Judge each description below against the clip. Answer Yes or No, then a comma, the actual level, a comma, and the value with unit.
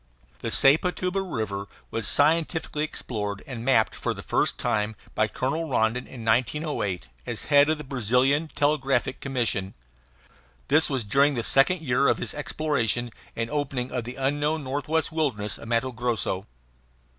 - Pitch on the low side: Yes, low, 130 Hz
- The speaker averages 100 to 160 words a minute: Yes, average, 150 wpm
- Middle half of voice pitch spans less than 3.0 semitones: No, average, 4.5 semitones